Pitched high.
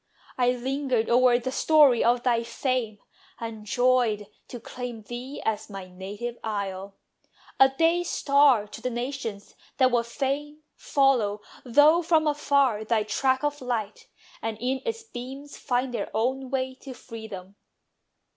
Yes: high, 245 Hz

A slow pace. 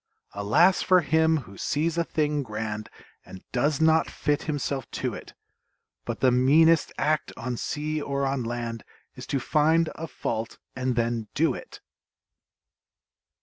No: average, 145 wpm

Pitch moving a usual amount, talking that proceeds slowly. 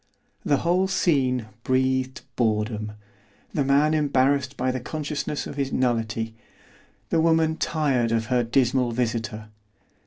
Yes: average, 3.8 semitones; slow, 125 wpm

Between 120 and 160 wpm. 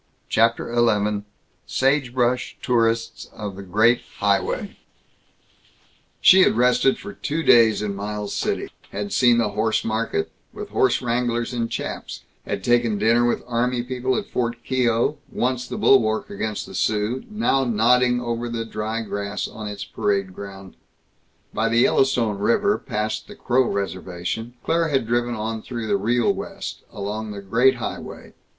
Yes: average, 150 wpm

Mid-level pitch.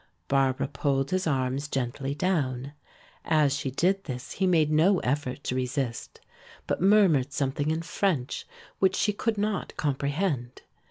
Yes: medium, 145 Hz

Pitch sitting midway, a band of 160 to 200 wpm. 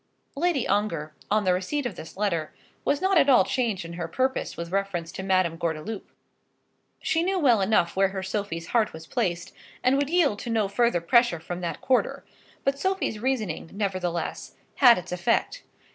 No: high, 200 Hz; average, 180 wpm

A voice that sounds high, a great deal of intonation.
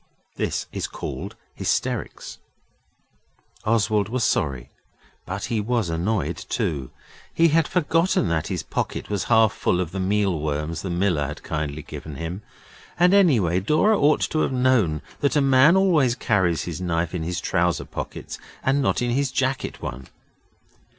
No: low, 100 Hz; wide, 8.0 semitones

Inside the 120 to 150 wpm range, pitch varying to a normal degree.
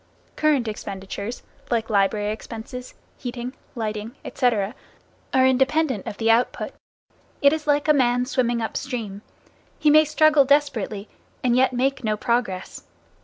Yes: slow, 135 wpm; average, 4.1 semitones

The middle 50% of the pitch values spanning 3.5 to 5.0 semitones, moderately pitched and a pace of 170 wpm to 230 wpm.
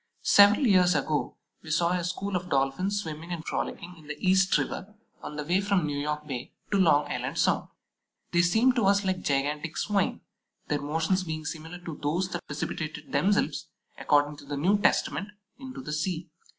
Yes: average, 4.2 semitones; medium, 170 Hz; average, 185 wpm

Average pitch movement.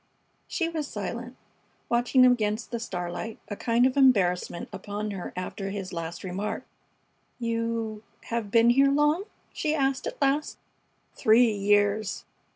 Yes: average, 3.9 semitones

